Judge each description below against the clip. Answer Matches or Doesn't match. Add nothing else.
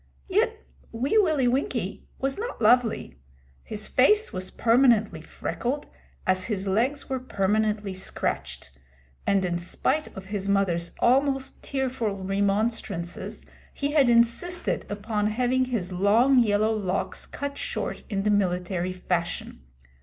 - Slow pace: Matches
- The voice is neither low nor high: Doesn't match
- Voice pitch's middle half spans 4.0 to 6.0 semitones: Matches